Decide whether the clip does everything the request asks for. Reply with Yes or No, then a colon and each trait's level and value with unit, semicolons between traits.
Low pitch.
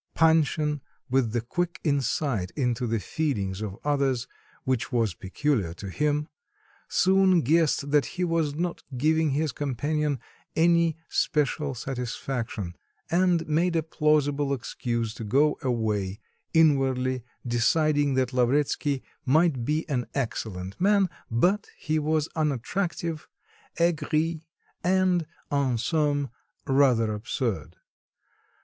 No: medium, 145 Hz